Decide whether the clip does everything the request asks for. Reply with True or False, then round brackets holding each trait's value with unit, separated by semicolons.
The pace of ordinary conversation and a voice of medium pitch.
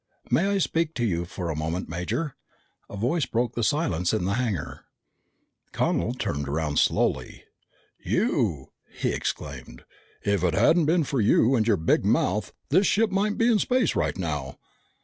False (165 wpm; 110 Hz)